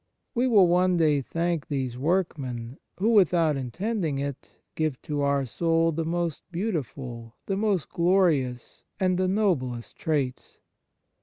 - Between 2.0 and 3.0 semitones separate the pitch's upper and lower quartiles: No, average, 5.2 semitones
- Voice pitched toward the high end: No, medium, 165 Hz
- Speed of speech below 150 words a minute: Yes, slow, 135 wpm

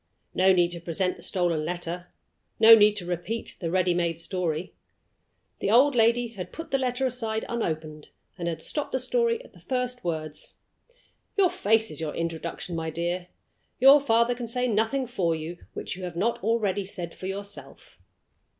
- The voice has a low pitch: No, high, 190 Hz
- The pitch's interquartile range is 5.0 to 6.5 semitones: Yes, wide, 5.6 semitones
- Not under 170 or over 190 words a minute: Yes, average, 175 wpm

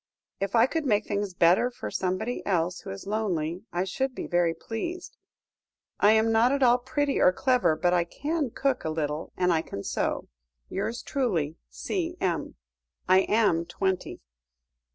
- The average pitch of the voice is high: Yes, high, 200 Hz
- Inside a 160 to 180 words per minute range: Yes, average, 165 wpm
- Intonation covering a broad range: Yes, wide, 6.3 semitones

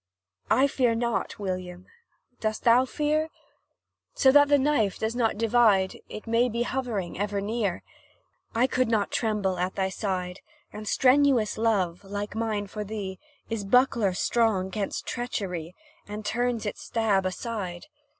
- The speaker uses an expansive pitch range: No, average, 3.8 semitones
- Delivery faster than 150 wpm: No, average, 145 wpm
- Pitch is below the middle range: No, high, 215 Hz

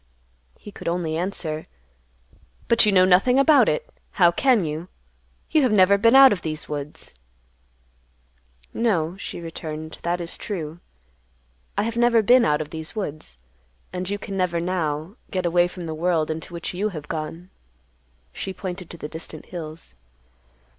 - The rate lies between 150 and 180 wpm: Yes, average, 160 wpm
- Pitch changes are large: No, average, 4.2 semitones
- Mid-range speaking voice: Yes, medium, 175 Hz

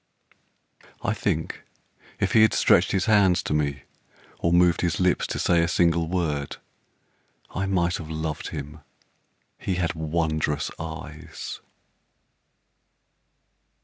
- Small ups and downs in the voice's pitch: Yes, narrow, 2.3 semitones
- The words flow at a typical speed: No, slow, 120 wpm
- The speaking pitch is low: Yes, very low, 85 Hz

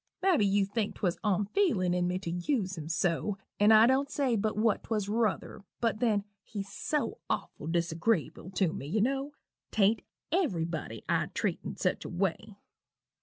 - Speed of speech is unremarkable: Yes, average, 170 wpm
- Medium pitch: No, high, 205 Hz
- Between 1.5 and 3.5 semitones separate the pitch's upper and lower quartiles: No, average, 4.3 semitones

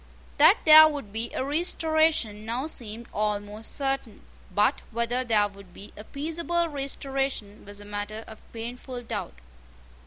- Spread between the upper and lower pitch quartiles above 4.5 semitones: Yes, average, 5.1 semitones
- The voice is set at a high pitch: Yes, high, 235 Hz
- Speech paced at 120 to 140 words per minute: Yes, slow, 135 wpm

